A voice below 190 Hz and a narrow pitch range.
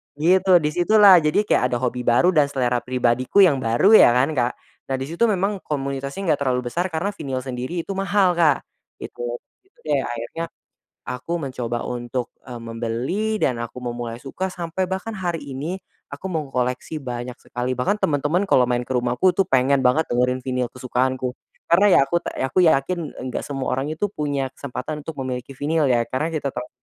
No: low, 135 Hz; wide, 5.5 semitones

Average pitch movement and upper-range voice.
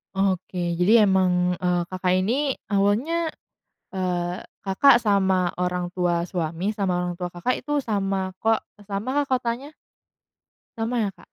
Yes: average, 4.5 semitones; high, 195 Hz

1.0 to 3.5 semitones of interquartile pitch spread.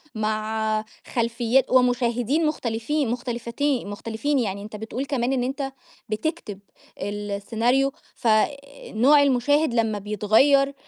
No: average, 3.9 semitones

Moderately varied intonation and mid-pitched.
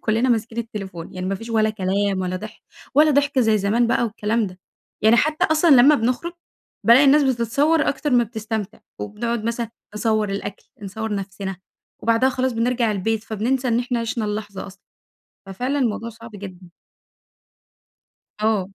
No: average, 3.2 semitones; high, 225 Hz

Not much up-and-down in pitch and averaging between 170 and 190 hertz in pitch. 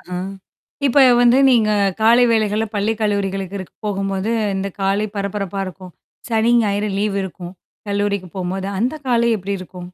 No: narrow, 2.3 semitones; high, 200 Hz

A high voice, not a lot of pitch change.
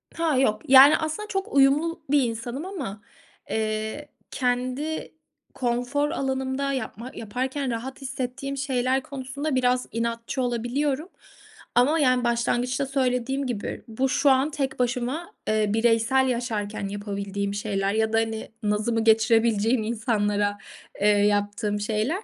No: high, 245 Hz; average, 3.7 semitones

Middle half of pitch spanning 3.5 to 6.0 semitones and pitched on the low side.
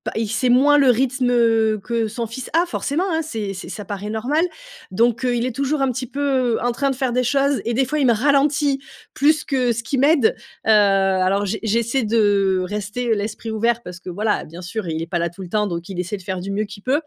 No: average, 4.6 semitones; high, 230 Hz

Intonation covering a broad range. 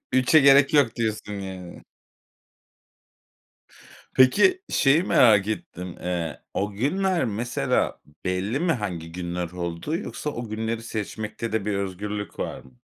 Yes: wide, 6.0 semitones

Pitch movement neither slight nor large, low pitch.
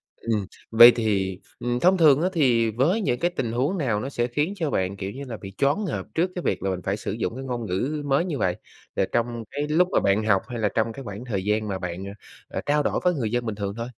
No: wide, 5.8 semitones; low, 120 Hz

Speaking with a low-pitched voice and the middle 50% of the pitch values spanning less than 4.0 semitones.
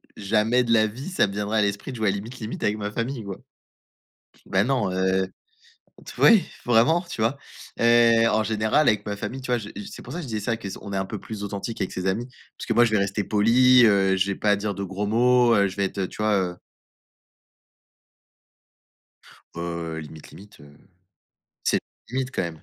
Yes: low, 105 Hz; average, 3.3 semitones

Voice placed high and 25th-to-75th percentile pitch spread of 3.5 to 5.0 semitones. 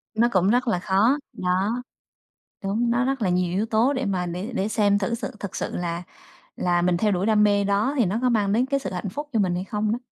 Yes: high, 205 Hz; average, 4.2 semitones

